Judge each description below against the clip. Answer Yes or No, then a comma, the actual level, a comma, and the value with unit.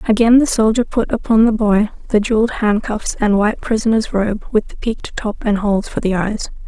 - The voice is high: Yes, high, 215 Hz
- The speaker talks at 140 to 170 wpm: No, fast, 205 wpm